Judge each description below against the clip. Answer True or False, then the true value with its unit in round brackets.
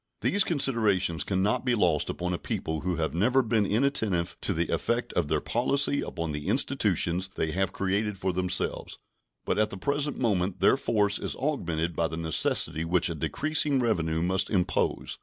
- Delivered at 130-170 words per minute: False (180 wpm)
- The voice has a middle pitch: False (95 Hz)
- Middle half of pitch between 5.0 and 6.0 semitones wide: True (5.6 semitones)